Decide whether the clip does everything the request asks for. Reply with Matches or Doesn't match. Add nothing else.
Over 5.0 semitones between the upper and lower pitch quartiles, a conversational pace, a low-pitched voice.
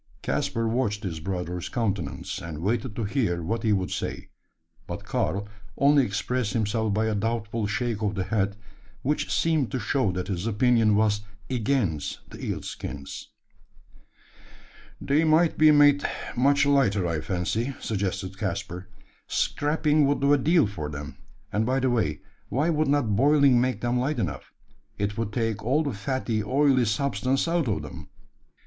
Matches